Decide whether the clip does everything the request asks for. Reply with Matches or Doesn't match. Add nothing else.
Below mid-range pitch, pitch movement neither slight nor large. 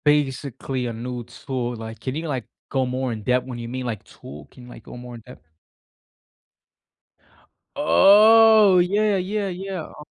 Doesn't match